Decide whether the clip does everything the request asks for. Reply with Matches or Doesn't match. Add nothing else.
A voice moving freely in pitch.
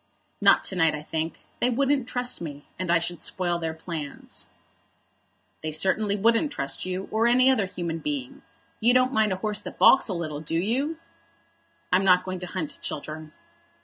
Matches